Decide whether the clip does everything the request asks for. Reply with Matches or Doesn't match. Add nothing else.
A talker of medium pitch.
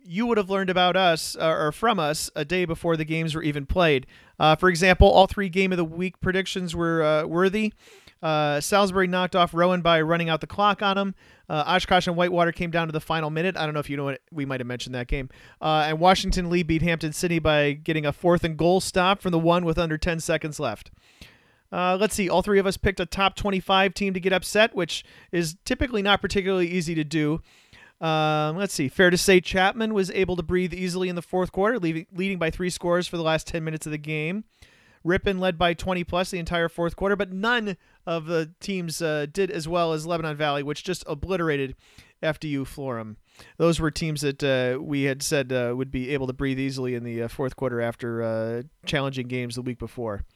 Matches